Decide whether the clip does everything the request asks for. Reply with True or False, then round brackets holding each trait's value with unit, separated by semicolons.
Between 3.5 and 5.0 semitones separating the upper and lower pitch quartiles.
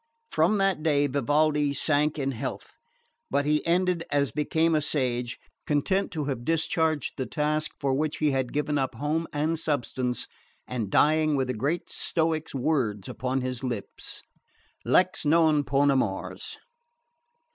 False (3.0 semitones)